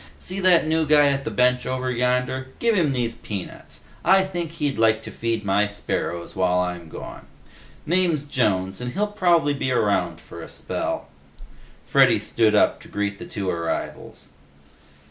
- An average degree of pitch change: No, wide, 7.3 semitones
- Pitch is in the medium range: No, low, 125 Hz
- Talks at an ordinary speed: Yes, average, 165 wpm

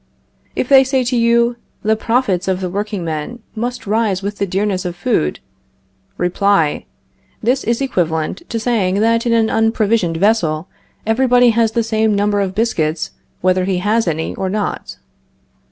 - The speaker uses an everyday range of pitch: Yes, average, 3.9 semitones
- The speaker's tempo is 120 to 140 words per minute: No, average, 155 wpm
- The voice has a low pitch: No, high, 210 Hz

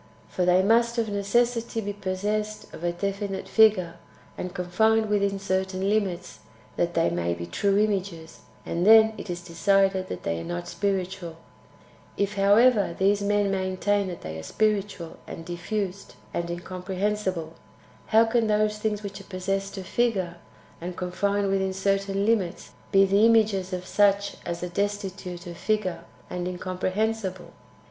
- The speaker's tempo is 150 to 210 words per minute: Yes, average, 155 wpm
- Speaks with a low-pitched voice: No, high, 195 Hz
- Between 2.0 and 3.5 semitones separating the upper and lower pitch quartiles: Yes, narrow, 2.5 semitones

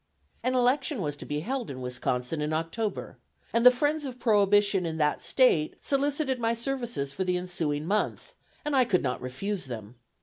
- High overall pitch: Yes, high, 200 Hz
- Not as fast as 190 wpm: Yes, average, 180 wpm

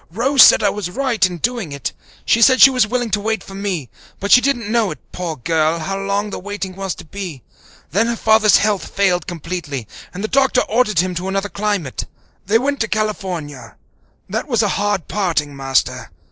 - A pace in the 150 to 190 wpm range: No, average, 200 wpm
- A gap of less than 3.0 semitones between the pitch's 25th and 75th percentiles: No, average, 4.2 semitones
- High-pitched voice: Yes, high, 200 Hz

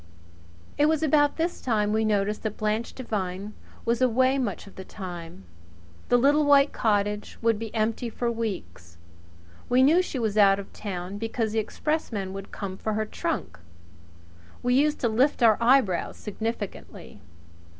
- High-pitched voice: Yes, high, 220 Hz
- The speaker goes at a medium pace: Yes, average, 160 wpm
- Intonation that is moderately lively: Yes, average, 4.2 semitones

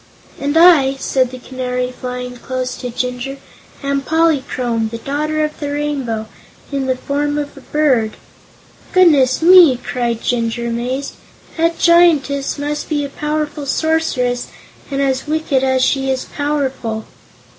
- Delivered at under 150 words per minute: Yes, average, 140 wpm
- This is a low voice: No, very high, 275 Hz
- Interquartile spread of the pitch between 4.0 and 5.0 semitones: No, average, 3.0 semitones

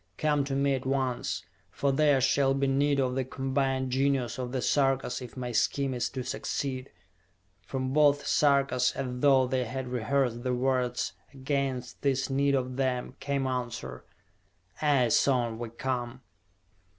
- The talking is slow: No, average, 155 wpm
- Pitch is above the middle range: No, low, 130 Hz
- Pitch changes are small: Yes, narrow, 1.6 semitones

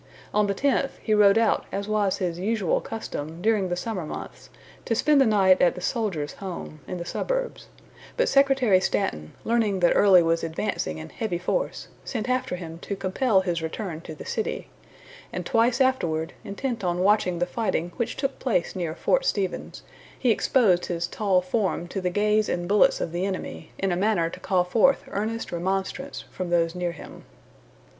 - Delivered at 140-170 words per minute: No, average, 185 wpm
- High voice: Yes, high, 195 Hz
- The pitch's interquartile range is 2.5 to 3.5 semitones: No, average, 4.3 semitones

